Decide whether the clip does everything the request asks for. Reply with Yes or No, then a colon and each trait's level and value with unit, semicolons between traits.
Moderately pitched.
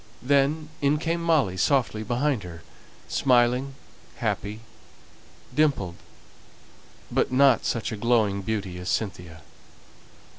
No: low, 120 Hz